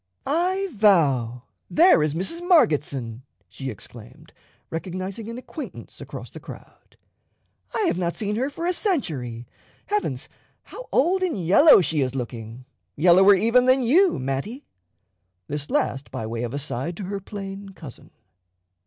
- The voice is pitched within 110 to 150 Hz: No, medium, 185 Hz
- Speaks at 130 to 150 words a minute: Yes, average, 145 wpm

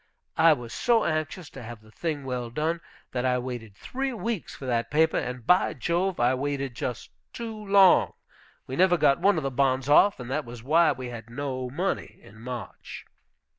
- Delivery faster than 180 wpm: Yes, average, 195 wpm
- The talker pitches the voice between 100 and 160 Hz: Yes, medium, 140 Hz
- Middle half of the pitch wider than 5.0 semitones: Yes, wide, 5.6 semitones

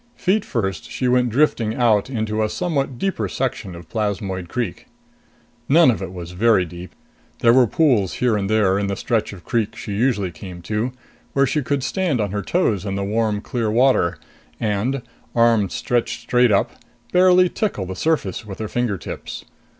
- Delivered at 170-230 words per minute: Yes, average, 185 wpm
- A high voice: No, low, 110 Hz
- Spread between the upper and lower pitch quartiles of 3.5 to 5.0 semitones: Yes, average, 4.2 semitones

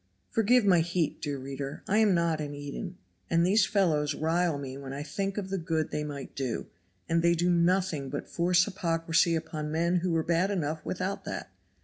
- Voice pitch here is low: No, medium, 165 Hz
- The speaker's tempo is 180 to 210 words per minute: Yes, average, 200 wpm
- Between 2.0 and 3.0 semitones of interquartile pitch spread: No, average, 3.5 semitones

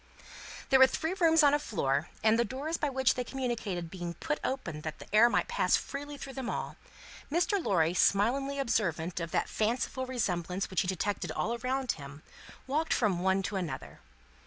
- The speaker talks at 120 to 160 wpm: No, average, 185 wpm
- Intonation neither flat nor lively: No, wide, 7.1 semitones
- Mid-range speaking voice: No, high, 235 Hz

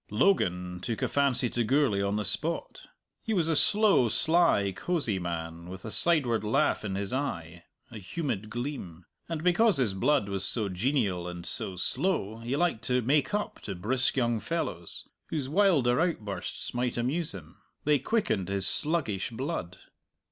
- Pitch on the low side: Yes, low, 120 Hz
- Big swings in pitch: Yes, wide, 7.5 semitones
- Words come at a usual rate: Yes, average, 165 wpm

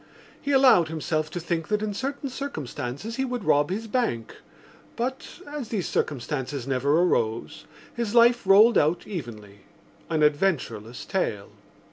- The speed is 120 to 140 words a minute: Yes, slow, 135 wpm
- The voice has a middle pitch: Yes, medium, 175 Hz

